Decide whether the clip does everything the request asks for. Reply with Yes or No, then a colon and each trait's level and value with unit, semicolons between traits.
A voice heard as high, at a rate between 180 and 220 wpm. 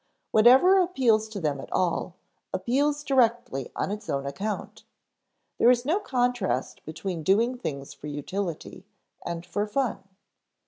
No: high, 210 Hz; slow, 135 wpm